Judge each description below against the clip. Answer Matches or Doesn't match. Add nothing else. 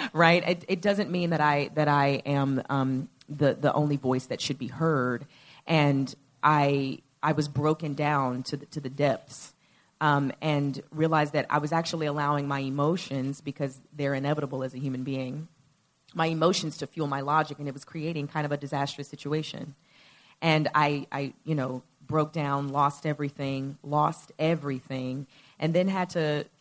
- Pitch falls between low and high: Matches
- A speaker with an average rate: Matches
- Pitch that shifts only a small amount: Matches